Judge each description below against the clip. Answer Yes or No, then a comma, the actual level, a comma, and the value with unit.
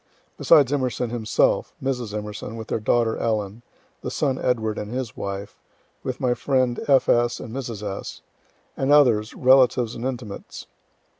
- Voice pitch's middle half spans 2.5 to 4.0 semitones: Yes, average, 3.1 semitones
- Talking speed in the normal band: Yes, average, 150 wpm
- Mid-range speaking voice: No, low, 120 Hz